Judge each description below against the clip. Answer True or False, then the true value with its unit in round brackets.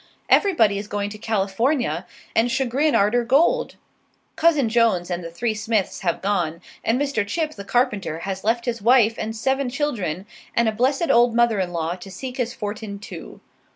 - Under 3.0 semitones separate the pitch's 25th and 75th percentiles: False (4.1 semitones)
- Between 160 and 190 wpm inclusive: True (180 wpm)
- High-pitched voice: True (225 Hz)